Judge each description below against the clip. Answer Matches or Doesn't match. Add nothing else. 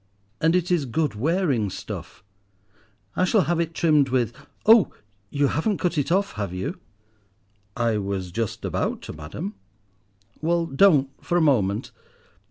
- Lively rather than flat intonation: Matches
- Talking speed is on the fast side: Doesn't match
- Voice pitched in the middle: Matches